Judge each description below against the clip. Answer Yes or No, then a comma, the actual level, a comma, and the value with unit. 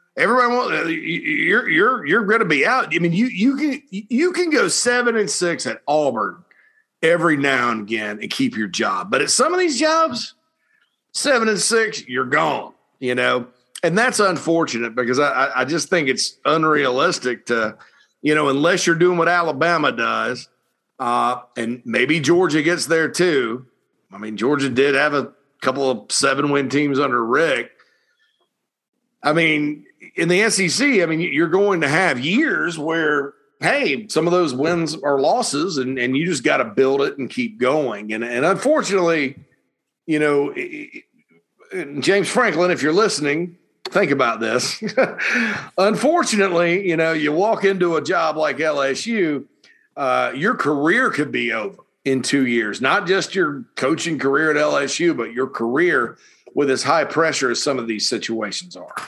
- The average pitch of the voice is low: No, medium, 165 Hz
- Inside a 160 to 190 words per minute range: Yes, average, 165 wpm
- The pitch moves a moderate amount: No, wide, 7.9 semitones